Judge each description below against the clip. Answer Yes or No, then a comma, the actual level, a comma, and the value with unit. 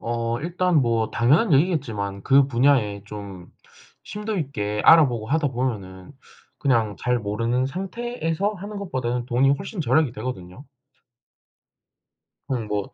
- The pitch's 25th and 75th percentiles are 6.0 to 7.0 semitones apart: Yes, wide, 6.5 semitones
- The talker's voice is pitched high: No, low, 125 Hz